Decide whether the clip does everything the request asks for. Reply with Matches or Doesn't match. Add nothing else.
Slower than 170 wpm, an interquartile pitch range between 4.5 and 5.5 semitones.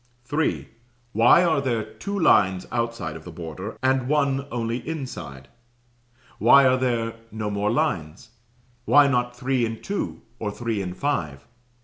Matches